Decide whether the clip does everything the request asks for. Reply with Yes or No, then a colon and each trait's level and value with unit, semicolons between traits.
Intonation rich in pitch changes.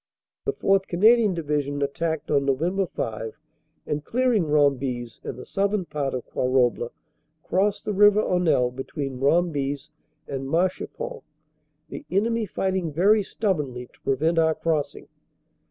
Yes: wide, 6.0 semitones